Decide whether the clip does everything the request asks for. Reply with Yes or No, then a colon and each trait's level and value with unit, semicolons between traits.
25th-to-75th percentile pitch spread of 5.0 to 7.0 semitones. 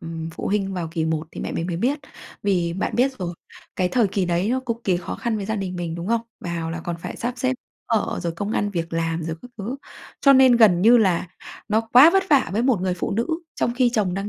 Yes: average, 5.3 semitones